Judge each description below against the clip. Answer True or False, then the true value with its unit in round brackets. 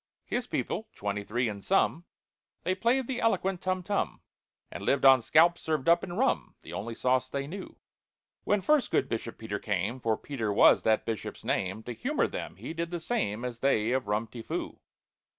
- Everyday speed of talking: True (190 wpm)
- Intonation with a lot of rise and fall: True (8.7 semitones)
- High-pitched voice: False (130 Hz)